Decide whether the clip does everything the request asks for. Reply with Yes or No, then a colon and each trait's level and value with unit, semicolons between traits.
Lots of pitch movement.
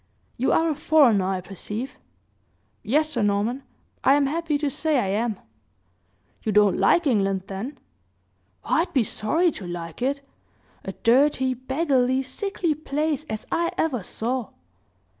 Yes: wide, 6.3 semitones